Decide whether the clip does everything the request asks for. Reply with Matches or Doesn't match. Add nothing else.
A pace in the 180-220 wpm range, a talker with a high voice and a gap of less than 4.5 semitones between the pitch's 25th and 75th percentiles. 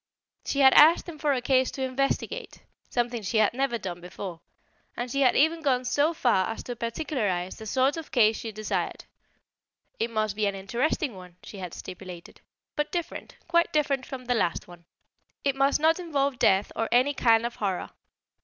Doesn't match